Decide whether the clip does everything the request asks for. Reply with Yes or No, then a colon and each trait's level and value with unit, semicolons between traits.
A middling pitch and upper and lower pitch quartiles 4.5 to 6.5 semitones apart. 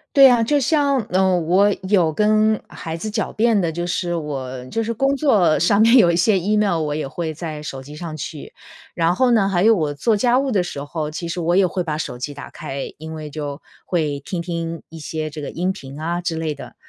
Yes: medium, 170 Hz; wide, 5.5 semitones